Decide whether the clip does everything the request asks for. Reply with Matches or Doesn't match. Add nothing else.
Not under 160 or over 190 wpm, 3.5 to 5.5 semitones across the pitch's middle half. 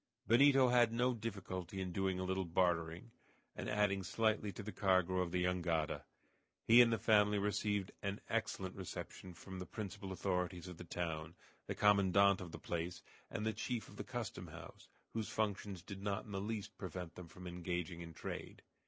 Doesn't match